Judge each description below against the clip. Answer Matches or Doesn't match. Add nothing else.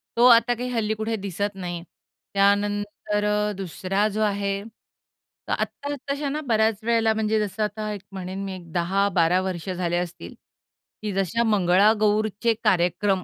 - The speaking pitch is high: Matches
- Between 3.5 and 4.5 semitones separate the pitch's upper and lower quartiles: Doesn't match